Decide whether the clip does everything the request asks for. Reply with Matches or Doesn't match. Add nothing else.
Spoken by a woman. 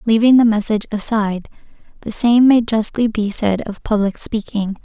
Matches